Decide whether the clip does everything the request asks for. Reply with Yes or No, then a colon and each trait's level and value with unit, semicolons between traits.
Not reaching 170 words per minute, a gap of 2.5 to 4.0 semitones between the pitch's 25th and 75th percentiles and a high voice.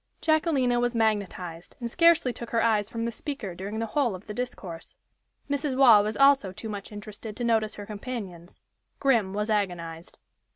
No: average, 175 wpm; average, 3.7 semitones; high, 220 Hz